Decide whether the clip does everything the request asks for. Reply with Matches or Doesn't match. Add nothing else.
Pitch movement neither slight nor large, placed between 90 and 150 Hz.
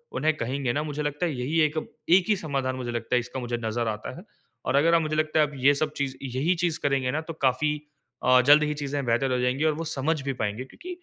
Matches